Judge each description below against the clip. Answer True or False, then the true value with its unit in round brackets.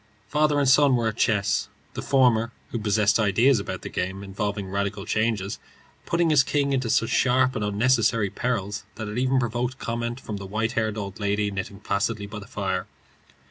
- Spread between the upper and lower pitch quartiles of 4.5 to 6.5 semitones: False (3.7 semitones)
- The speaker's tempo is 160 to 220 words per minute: True (185 wpm)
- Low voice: True (110 Hz)